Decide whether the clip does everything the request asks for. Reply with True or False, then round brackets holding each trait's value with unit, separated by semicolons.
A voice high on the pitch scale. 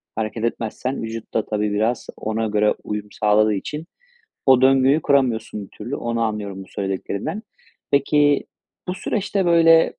False (115 Hz)